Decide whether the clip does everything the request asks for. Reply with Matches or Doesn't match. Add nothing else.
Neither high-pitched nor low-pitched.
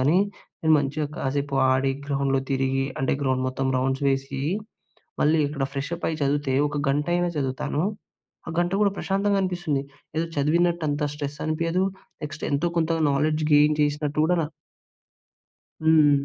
Matches